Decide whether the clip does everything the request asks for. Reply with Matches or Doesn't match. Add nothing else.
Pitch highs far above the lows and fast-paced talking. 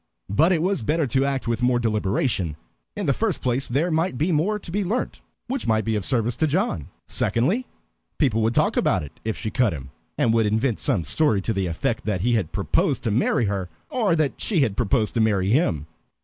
Matches